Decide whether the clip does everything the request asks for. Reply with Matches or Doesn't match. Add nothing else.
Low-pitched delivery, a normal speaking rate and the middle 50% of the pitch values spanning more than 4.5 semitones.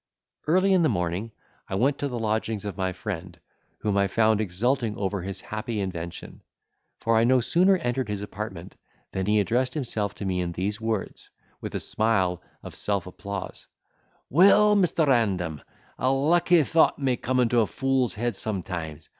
Matches